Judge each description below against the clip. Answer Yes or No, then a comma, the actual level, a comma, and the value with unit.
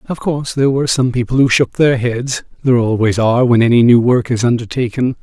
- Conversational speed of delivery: No, fast, 220 wpm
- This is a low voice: Yes, low, 125 Hz